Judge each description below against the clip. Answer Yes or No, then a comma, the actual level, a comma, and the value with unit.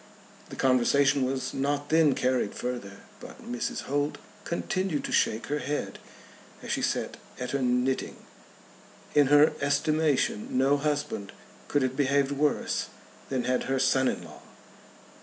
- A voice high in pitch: No, low, 135 Hz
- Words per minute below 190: Yes, average, 140 wpm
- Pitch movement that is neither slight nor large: No, narrow, 2.2 semitones